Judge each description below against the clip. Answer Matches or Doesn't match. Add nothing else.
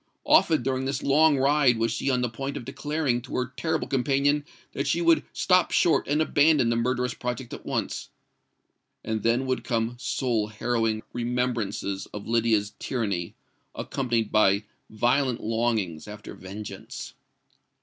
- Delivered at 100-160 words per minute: Matches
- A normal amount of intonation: Matches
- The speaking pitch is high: Doesn't match